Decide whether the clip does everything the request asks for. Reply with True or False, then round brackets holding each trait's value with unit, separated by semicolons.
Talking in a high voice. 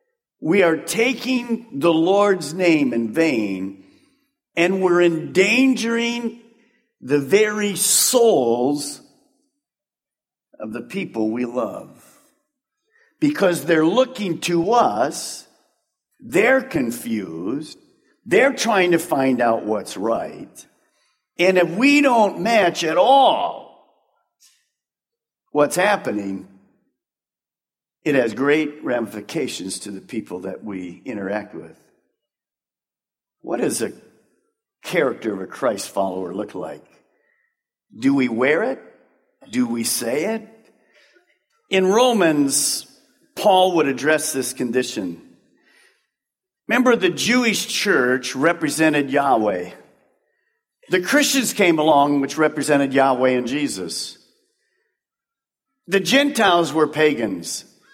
True (195 Hz)